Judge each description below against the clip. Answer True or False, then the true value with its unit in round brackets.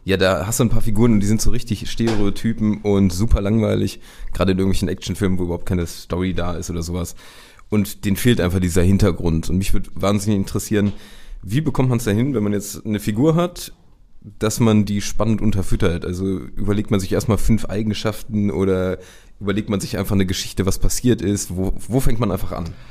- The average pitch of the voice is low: True (100 Hz)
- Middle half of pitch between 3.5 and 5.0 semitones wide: False (2.6 semitones)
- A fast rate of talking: True (205 wpm)